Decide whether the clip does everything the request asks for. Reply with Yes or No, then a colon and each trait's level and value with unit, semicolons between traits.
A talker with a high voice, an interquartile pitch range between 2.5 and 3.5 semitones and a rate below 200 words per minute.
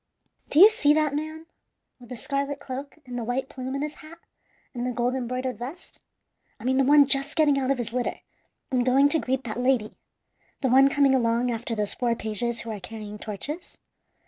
No: very high, 260 Hz; average, 2.8 semitones; fast, 205 wpm